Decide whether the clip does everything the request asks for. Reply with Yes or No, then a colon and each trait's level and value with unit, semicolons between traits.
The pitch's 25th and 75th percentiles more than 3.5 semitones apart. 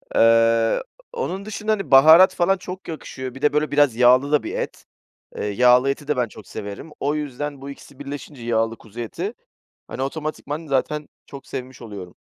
Yes: average, 4.0 semitones